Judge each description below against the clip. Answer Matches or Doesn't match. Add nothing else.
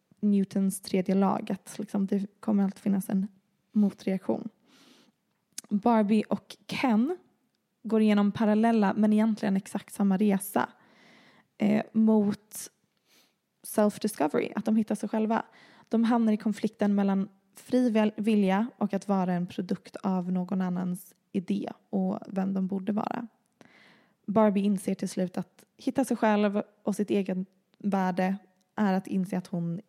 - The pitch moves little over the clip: Matches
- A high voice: Matches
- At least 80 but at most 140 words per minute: Matches